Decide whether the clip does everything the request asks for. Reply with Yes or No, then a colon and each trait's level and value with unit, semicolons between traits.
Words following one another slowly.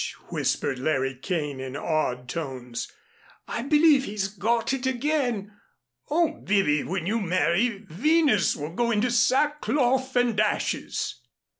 Yes: slow, 125 wpm